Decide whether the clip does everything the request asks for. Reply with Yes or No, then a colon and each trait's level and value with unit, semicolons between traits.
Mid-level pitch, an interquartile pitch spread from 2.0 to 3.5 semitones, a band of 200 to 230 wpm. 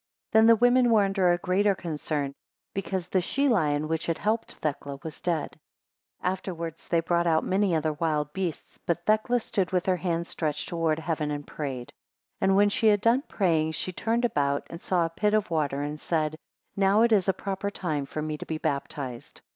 No: medium, 170 Hz; average, 4.4 semitones; fast, 205 wpm